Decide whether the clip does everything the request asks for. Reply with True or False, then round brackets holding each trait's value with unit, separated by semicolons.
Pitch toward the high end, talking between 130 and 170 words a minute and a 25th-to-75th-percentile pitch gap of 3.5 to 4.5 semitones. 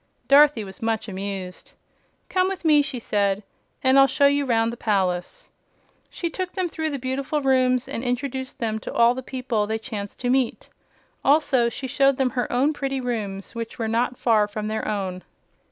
False (245 Hz; 185 wpm; 4.0 semitones)